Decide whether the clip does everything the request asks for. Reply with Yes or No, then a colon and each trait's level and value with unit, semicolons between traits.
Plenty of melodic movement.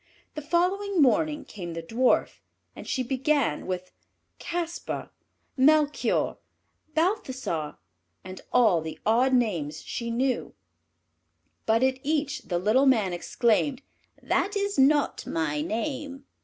Yes: wide, 7.4 semitones